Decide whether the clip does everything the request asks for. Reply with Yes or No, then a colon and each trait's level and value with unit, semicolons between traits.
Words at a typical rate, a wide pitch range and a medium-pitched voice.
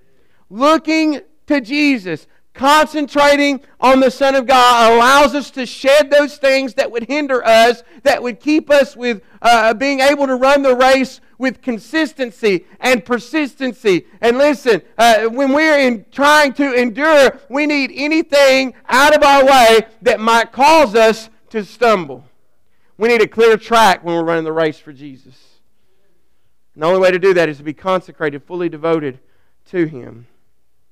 No: average, 165 wpm; wide, 6.4 semitones; high, 245 Hz